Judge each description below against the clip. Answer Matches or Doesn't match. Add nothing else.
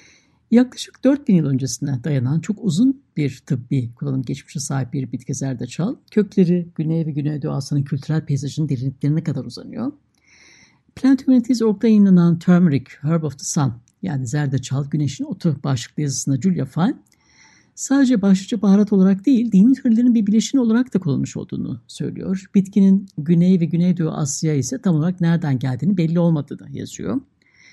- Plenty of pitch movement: Matches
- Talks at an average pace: Doesn't match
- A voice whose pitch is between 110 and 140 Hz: Doesn't match